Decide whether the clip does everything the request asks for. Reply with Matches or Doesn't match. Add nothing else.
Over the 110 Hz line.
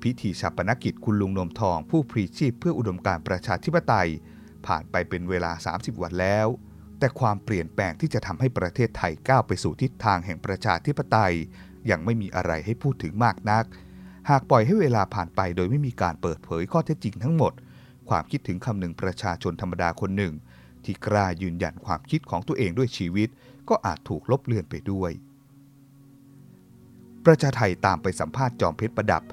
Doesn't match